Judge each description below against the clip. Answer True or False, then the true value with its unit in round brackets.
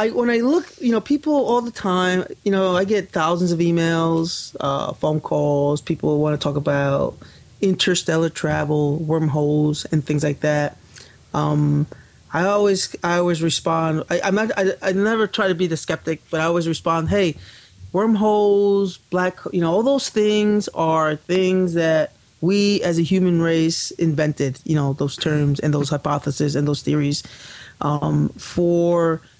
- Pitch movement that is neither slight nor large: True (4.2 semitones)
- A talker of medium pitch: True (165 Hz)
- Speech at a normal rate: True (165 wpm)